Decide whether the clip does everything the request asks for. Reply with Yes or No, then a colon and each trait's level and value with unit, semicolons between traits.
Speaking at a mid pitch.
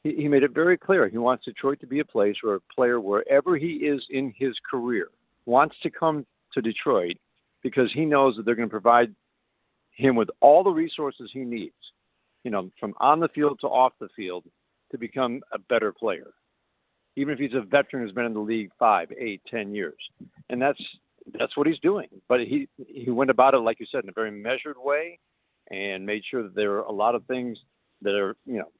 No: low, 130 Hz